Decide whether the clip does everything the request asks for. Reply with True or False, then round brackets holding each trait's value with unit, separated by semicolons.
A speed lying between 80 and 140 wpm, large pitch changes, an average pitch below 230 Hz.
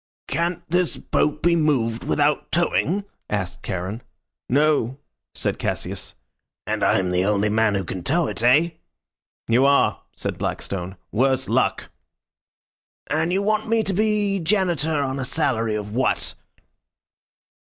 True (135 wpm; 7.6 semitones; 140 Hz)